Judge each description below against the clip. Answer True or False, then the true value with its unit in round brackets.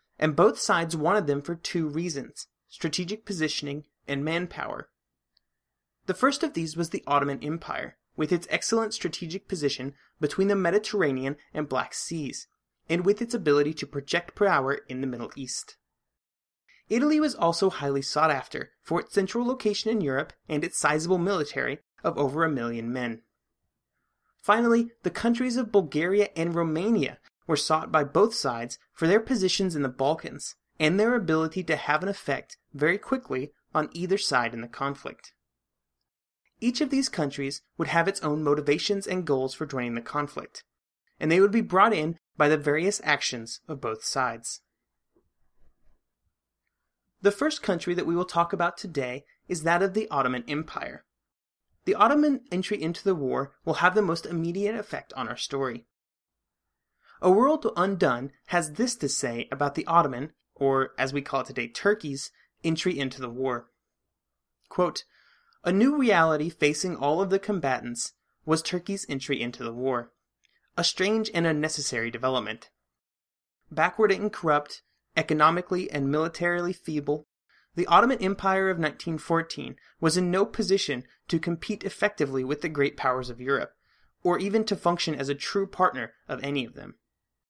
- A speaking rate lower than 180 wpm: True (160 wpm)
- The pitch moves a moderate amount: False (5.7 semitones)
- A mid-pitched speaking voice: True (160 Hz)